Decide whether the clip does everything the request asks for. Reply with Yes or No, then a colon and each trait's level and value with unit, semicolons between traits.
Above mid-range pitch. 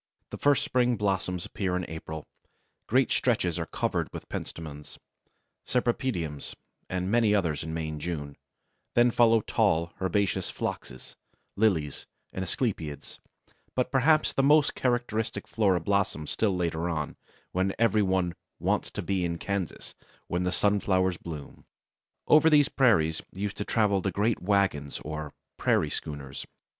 No: very low, 95 Hz